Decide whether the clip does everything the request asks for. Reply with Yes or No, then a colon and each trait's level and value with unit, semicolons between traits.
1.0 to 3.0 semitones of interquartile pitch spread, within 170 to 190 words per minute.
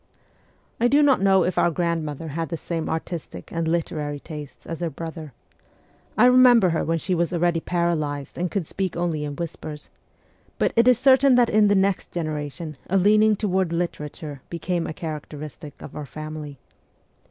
No: average, 3.8 semitones; average, 175 wpm